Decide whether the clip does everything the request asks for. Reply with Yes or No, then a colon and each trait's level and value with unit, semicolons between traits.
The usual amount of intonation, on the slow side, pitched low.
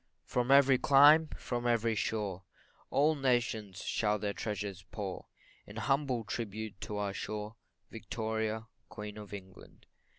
Yes: average, 3.0 semitones; slow, 130 wpm; low, 110 Hz